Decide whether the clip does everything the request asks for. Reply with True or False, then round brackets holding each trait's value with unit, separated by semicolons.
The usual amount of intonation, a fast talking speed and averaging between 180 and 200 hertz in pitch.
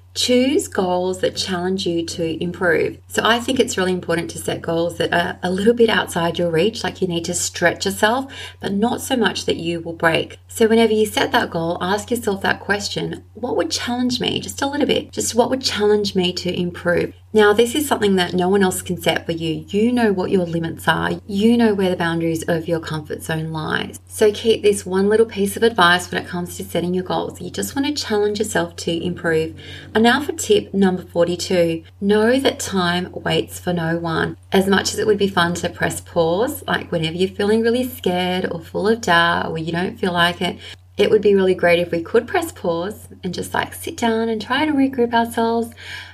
True (4.8 semitones; 225 wpm; 185 Hz)